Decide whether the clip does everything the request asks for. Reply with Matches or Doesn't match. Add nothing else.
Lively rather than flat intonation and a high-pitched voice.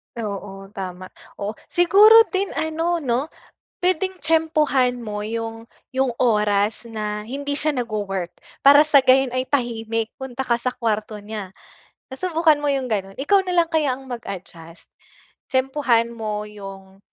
Matches